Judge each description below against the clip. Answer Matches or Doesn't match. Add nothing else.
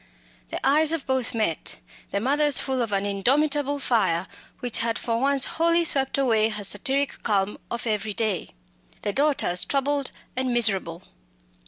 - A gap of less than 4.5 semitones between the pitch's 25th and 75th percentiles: Doesn't match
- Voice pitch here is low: Doesn't match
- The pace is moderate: Matches